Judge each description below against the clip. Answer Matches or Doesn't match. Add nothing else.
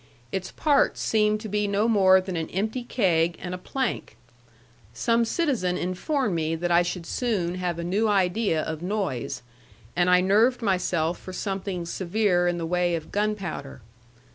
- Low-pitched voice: Doesn't match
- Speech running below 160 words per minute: Doesn't match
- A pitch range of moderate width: Matches